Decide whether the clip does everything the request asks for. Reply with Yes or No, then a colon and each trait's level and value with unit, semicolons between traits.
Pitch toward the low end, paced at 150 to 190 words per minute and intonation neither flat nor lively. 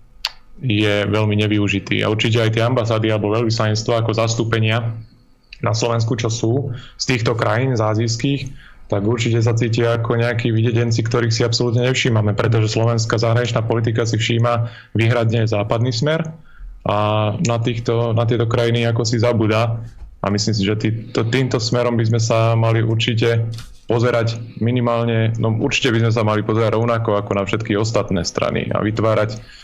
No: low, 115 Hz; average, 160 wpm; narrow, 1.4 semitones